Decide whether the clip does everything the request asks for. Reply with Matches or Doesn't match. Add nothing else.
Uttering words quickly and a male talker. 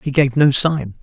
Matches